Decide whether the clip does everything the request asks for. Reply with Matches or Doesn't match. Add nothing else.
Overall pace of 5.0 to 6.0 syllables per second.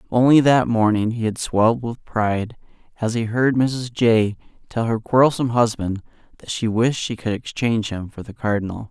Matches